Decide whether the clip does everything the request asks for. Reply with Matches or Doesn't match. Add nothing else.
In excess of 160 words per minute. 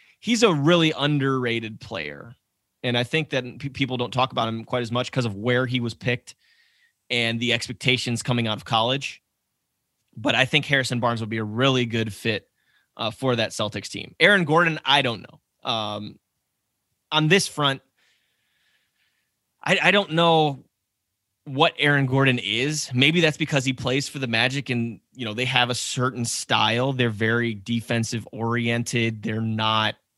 Matches